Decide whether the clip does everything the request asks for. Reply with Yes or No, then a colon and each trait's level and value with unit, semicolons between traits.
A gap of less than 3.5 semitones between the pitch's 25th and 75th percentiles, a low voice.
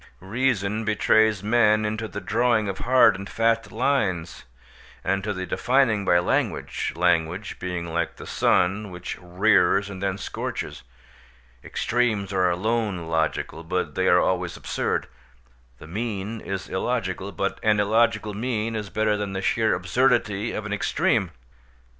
Yes: average, 3.1 semitones; low, 105 Hz